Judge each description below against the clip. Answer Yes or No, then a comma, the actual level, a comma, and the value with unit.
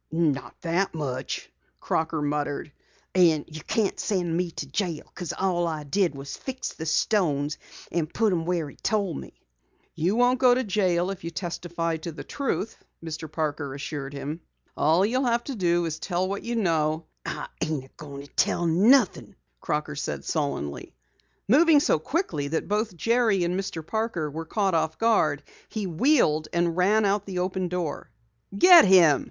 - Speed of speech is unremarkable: Yes, average, 175 wpm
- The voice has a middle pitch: Yes, medium, 170 Hz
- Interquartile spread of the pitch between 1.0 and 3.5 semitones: No, average, 4.6 semitones